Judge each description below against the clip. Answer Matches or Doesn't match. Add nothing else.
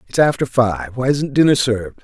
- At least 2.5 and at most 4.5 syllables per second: Doesn't match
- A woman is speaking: Doesn't match